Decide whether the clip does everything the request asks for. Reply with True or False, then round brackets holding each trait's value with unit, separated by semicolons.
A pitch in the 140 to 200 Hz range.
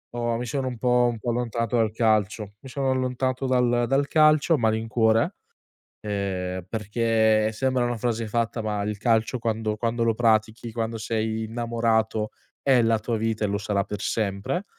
False (115 Hz)